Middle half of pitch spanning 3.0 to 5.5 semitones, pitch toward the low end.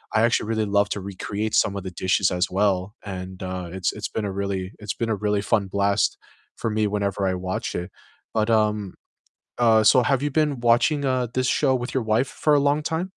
Yes: average, 3.7 semitones; low, 105 Hz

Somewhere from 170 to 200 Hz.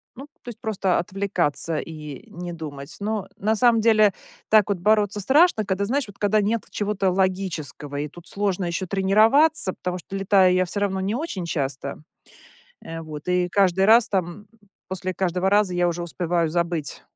Yes: high, 190 Hz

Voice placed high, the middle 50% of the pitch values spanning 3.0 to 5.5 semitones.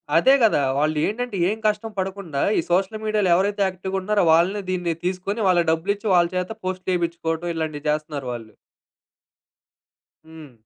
No: medium, 180 Hz; average, 3.8 semitones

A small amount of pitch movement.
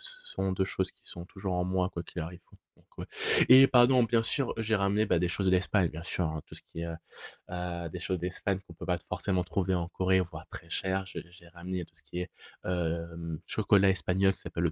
Yes: narrow, 2.1 semitones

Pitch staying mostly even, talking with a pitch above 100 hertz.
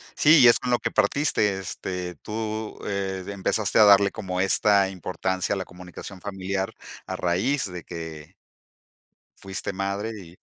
No: narrow, 2.3 semitones; very low, 95 Hz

